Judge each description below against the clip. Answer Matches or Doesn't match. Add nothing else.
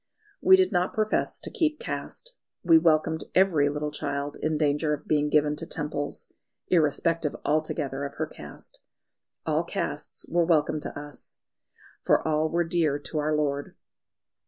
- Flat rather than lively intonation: Matches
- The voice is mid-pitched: Matches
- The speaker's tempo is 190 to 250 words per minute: Doesn't match